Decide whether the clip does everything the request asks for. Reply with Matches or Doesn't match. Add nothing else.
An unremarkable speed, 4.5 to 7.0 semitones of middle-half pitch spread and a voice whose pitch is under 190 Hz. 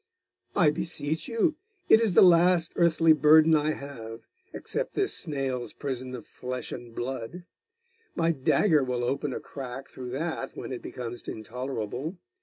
Matches